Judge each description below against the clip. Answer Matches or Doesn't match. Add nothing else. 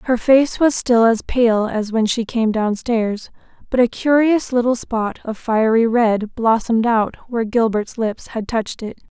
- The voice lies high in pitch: Matches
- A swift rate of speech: Doesn't match